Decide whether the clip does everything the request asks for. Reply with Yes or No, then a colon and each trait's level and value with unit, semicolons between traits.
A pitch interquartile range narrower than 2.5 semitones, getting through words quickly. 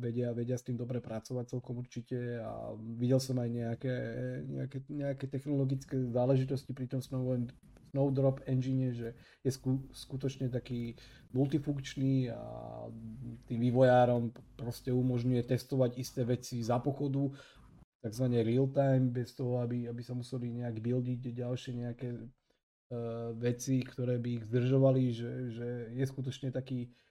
No: narrow, 1.5 semitones; average, 140 wpm